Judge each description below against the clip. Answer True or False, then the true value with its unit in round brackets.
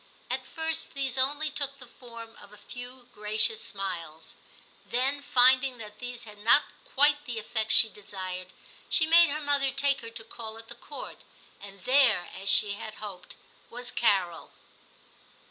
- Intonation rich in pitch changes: False (4.7 semitones)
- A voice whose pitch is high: True (235 Hz)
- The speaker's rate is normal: True (165 wpm)